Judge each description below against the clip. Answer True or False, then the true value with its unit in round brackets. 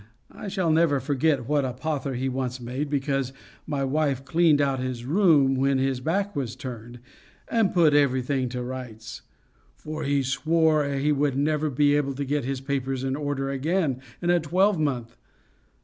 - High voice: False (140 Hz)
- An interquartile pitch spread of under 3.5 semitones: True (2.8 semitones)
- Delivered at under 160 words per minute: False (175 wpm)